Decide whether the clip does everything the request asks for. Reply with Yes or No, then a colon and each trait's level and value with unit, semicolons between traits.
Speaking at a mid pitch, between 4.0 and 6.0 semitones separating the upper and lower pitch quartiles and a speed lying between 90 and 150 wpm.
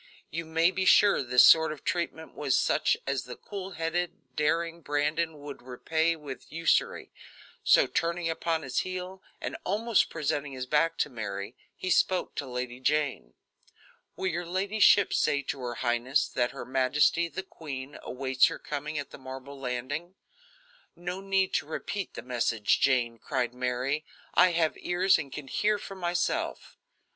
No: medium, 150 Hz; average, 4.9 semitones; average, 160 wpm